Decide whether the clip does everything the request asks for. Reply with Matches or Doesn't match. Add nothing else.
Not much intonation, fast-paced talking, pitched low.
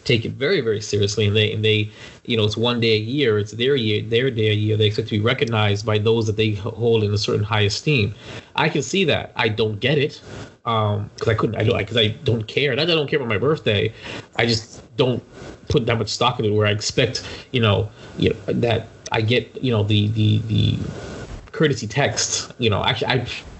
Matches